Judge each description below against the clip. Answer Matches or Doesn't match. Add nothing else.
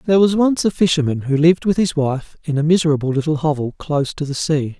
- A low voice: Doesn't match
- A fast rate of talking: Matches